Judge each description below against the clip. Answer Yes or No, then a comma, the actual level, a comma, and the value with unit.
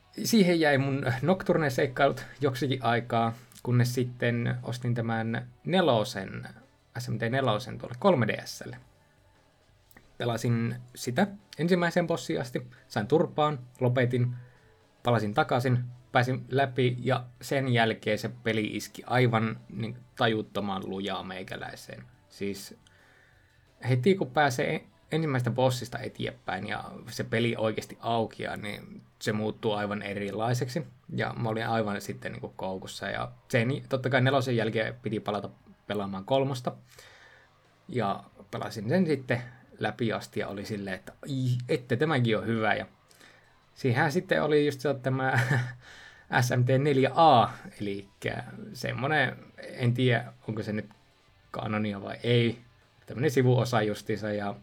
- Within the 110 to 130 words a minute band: Yes, average, 120 wpm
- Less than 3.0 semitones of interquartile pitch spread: No, average, 3.3 semitones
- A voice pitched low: Yes, low, 120 Hz